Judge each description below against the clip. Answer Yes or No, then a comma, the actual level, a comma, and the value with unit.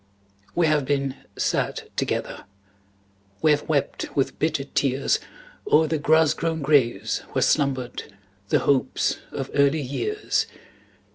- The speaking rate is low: Yes, slow, 125 wpm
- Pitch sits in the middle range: Yes, medium, 145 Hz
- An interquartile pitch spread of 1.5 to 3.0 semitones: Yes, narrow, 2.5 semitones